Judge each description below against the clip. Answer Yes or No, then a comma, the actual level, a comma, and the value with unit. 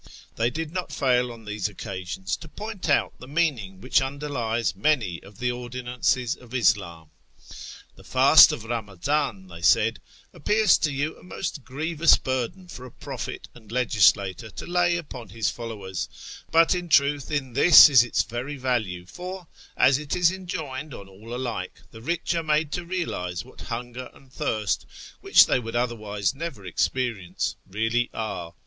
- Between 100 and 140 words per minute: No, average, 165 wpm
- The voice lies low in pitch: Yes, low, 125 Hz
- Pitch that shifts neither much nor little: No, wide, 5.8 semitones